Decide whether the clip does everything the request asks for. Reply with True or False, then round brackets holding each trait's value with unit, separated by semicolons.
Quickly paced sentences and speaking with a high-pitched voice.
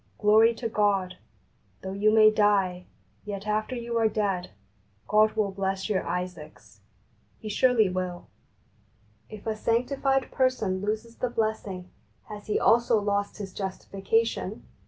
False (140 wpm; 210 Hz)